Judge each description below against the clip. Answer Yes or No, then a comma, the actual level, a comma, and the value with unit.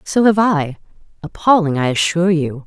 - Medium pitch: Yes, medium, 170 Hz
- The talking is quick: No, average, 160 wpm